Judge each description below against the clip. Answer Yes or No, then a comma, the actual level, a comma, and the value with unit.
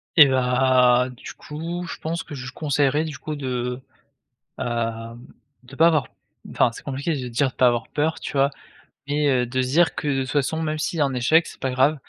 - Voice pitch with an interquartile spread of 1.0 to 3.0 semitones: No, average, 3.5 semitones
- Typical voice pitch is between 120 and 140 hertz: Yes, low, 135 Hz